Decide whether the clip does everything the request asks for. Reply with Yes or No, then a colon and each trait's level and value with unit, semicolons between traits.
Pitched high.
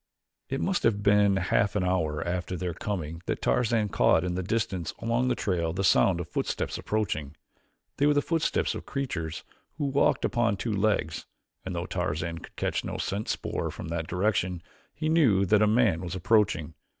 No: very low, 95 Hz